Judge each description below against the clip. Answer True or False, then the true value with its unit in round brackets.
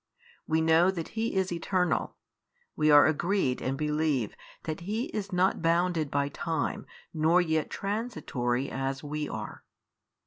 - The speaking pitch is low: False (160 Hz)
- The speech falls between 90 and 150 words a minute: True (140 wpm)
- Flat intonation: False (3.8 semitones)